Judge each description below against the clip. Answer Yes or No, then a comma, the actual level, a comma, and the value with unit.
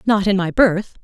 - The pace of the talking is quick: Yes, fast, 230 wpm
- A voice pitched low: No, high, 200 Hz